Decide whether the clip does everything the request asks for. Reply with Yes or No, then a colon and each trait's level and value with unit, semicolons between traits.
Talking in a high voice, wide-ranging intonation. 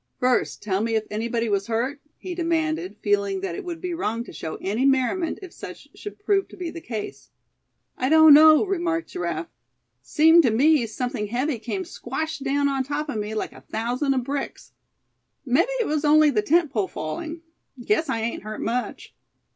Yes: very high, 275 Hz; wide, 6.3 semitones